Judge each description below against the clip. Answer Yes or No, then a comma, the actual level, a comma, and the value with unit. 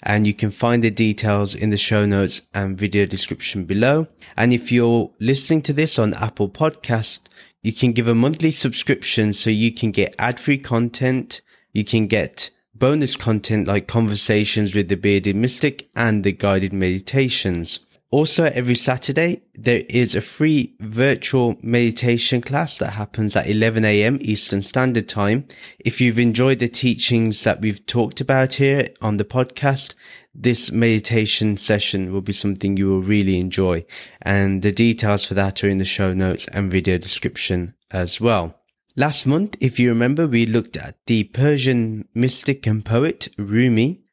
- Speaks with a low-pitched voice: Yes, low, 115 Hz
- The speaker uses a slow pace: No, average, 165 wpm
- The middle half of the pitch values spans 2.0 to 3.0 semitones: No, average, 3.8 semitones